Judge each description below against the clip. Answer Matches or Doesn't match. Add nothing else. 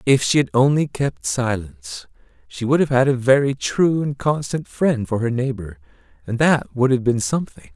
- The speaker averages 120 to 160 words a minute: Doesn't match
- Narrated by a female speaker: Doesn't match